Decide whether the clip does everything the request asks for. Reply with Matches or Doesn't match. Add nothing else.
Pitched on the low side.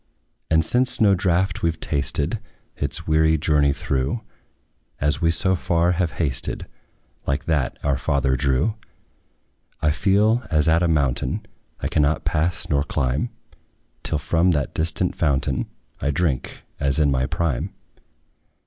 Matches